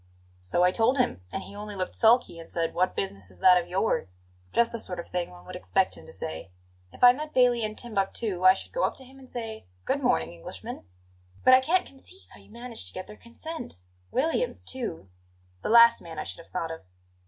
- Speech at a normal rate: No, fast, 230 wpm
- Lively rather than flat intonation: Yes, wide, 6.7 semitones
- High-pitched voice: Yes, high, 210 Hz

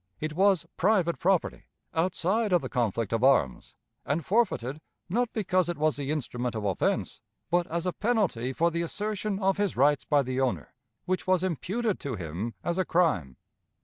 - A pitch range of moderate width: No, wide, 6.5 semitones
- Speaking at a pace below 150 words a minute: No, average, 180 wpm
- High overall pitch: No, medium, 170 Hz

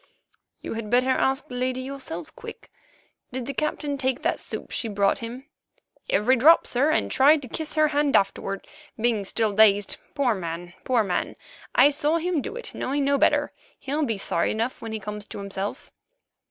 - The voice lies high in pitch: Yes, very high, 255 Hz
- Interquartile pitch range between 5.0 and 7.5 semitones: Yes, average, 5.3 semitones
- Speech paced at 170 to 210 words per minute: Yes, average, 185 wpm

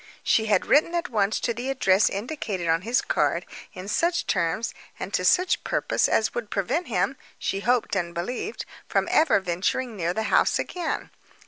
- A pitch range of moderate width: No, wide, 6.1 semitones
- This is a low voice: No, high, 220 Hz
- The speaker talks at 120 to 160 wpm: No, average, 180 wpm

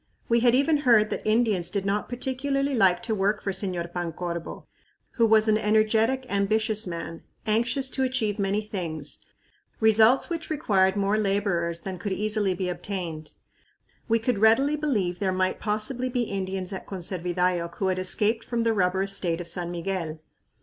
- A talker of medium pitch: No, high, 205 Hz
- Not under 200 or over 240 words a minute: No, average, 165 wpm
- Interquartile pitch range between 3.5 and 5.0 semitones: Yes, average, 3.8 semitones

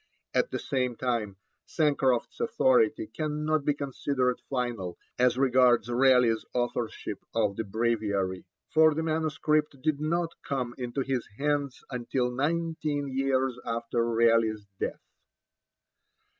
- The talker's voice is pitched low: Yes, low, 130 Hz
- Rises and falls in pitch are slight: No, average, 4.1 semitones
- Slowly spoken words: Yes, slow, 115 wpm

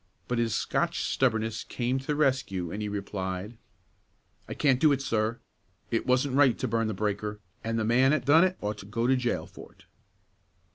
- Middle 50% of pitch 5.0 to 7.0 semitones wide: No, average, 3.8 semitones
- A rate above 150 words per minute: Yes, average, 200 wpm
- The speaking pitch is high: No, low, 115 Hz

